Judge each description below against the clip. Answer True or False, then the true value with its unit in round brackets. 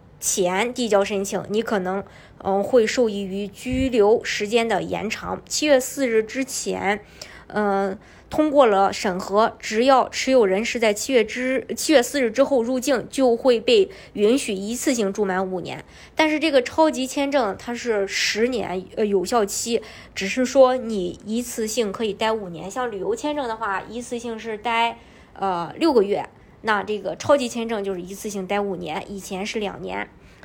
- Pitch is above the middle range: True (225 Hz)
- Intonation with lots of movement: False (4.3 semitones)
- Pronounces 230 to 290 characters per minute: True (250 characters per minute)